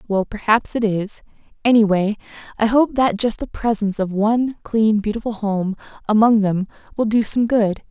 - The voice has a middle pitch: No, high, 215 Hz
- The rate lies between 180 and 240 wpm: No, average, 165 wpm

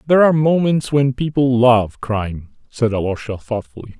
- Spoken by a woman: No, male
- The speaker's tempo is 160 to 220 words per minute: No, average, 150 wpm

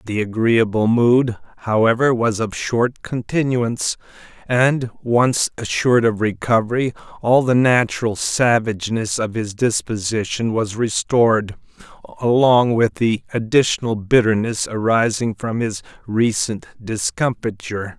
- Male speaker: Yes, male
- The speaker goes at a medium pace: No, slow, 105 wpm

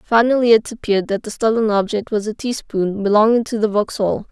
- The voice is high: Yes, high, 215 Hz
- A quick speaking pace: No, average, 195 wpm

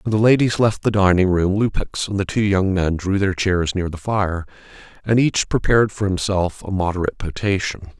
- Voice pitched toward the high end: No, very low, 95 Hz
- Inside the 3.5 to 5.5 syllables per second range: Yes, 5.2 syllables/s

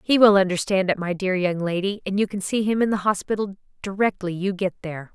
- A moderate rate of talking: No, fast, 235 wpm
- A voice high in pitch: Yes, high, 195 Hz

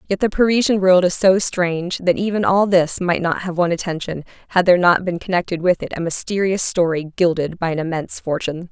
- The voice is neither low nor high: Yes, medium, 175 Hz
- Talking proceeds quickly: Yes, fast, 215 wpm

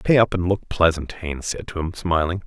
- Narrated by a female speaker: No, male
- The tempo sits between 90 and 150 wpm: No, fast, 245 wpm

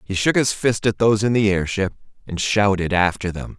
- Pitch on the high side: No, low, 100 Hz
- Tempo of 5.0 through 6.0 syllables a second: Yes, 5.4 syllables/s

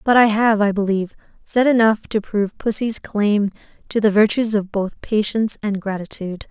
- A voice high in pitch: Yes, high, 210 Hz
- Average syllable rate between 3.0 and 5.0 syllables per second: No, 5.3 syllables/s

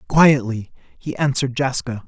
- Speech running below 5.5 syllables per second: Yes, 5.0 syllables/s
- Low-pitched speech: Yes, low, 130 Hz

